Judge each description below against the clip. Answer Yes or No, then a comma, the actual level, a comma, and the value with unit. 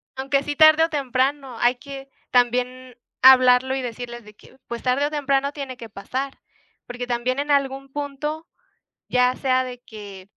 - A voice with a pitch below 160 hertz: No, very high, 260 Hz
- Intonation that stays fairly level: Yes, narrow, 2.0 semitones